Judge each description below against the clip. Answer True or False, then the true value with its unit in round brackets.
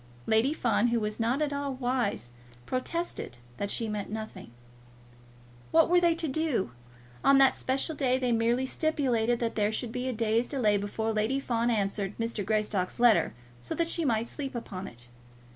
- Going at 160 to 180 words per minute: True (175 wpm)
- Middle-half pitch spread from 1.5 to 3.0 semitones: False (4.0 semitones)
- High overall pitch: True (235 Hz)